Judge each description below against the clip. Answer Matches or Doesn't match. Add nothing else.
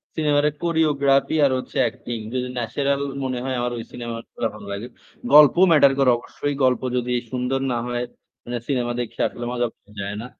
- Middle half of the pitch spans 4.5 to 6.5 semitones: Doesn't match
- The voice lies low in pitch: Matches